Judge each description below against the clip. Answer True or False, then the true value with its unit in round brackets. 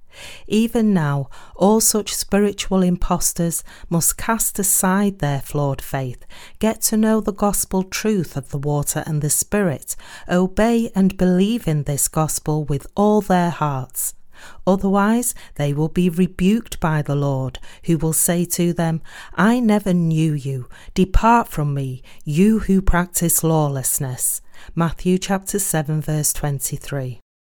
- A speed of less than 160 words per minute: True (140 wpm)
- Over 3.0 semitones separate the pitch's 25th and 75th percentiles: True (5.3 semitones)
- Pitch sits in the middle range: True (175 Hz)